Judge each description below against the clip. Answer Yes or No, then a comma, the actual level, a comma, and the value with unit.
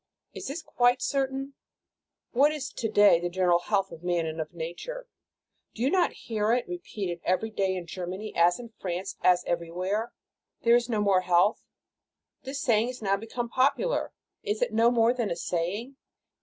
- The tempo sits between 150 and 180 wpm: Yes, average, 175 wpm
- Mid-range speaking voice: No, high, 215 Hz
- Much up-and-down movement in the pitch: Yes, wide, 5.7 semitones